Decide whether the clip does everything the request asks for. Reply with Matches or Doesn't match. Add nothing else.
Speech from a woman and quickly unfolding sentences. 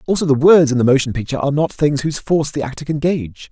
Doesn't match